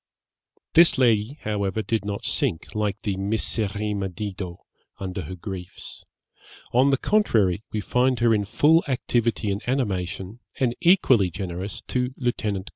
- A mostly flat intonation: No, average, 4.2 semitones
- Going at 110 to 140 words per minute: Yes, slow, 135 wpm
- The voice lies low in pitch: Yes, low, 105 Hz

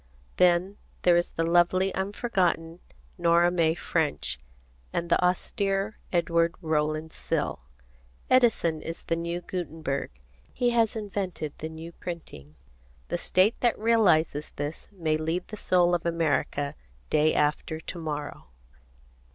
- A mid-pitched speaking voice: Yes, medium, 170 Hz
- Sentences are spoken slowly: Yes, slow, 125 wpm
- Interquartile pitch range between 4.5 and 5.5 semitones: No, average, 2.7 semitones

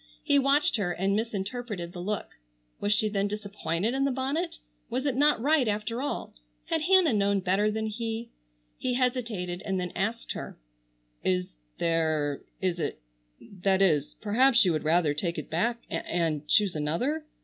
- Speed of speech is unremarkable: Yes, average, 165 wpm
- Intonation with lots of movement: Yes, wide, 6.0 semitones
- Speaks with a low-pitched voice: No, high, 210 Hz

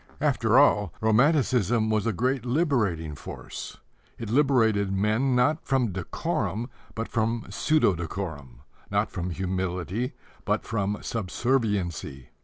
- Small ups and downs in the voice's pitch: No, average, 4.8 semitones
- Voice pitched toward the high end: No, low, 110 Hz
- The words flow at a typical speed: No, slow, 115 wpm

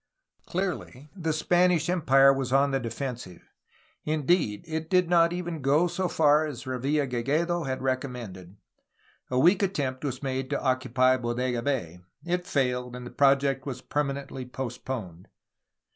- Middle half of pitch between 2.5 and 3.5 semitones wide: No, average, 4.0 semitones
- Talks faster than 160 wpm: No, average, 150 wpm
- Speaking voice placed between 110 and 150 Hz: Yes, low, 135 Hz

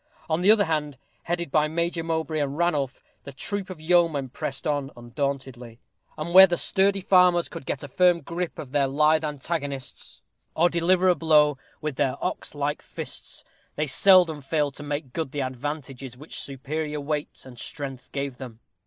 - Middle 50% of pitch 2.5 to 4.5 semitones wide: Yes, average, 3.7 semitones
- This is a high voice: No, medium, 150 Hz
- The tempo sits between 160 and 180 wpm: Yes, average, 175 wpm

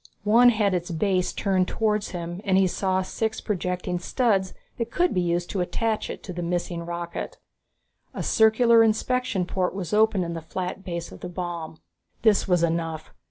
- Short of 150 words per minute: No, average, 180 wpm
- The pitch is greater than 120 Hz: Yes, medium, 185 Hz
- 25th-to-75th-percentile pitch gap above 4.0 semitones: No, average, 3.6 semitones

